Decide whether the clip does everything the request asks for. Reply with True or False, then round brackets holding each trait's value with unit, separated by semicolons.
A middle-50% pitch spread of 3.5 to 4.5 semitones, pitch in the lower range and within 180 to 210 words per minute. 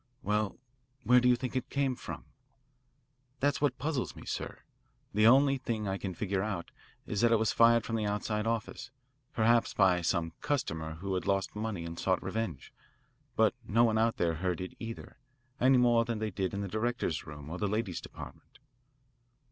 True (3.8 semitones; 110 Hz; 190 wpm)